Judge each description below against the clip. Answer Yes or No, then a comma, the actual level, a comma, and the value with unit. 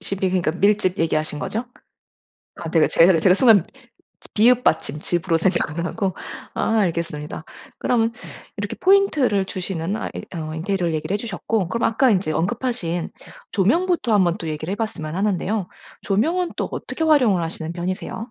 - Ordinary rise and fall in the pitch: Yes, average, 5.0 semitones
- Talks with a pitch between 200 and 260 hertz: No, high, 190 Hz